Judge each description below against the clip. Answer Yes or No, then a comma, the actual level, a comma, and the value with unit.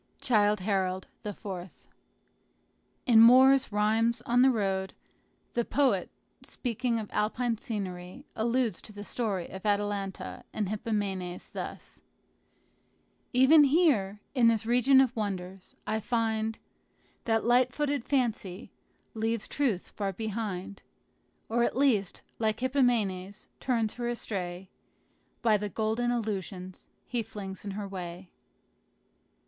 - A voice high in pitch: Yes, high, 220 Hz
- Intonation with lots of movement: No, average, 3.7 semitones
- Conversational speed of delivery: No, slow, 120 wpm